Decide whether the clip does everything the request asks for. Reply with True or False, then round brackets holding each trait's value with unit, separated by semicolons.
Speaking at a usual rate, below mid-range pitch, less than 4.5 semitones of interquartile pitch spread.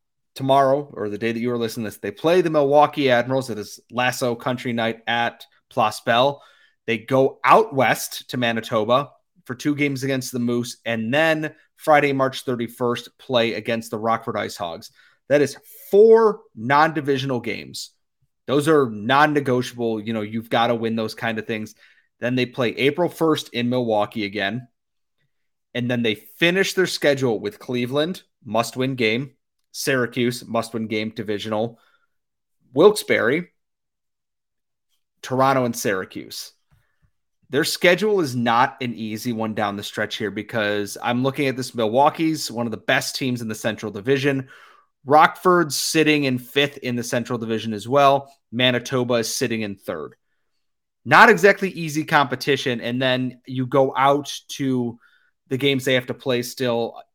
True (155 wpm; 125 Hz; 3.7 semitones)